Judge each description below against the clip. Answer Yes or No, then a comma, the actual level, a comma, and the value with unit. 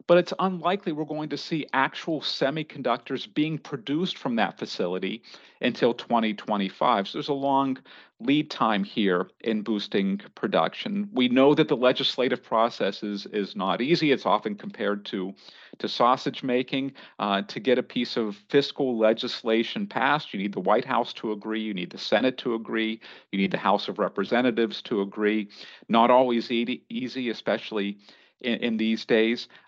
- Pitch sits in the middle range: No, low, 125 Hz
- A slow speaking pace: No, average, 165 wpm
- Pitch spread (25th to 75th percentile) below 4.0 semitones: No, average, 4.8 semitones